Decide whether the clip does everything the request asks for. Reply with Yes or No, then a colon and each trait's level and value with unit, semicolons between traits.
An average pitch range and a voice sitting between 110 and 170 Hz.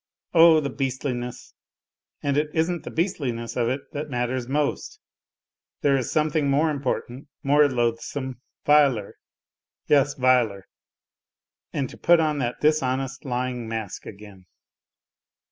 Yes: average, 3.4 semitones; low, 135 Hz